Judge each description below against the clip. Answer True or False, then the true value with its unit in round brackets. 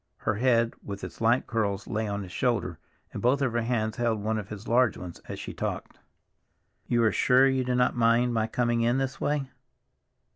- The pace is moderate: False (210 wpm)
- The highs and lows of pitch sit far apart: False (2.4 semitones)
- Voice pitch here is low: True (115 Hz)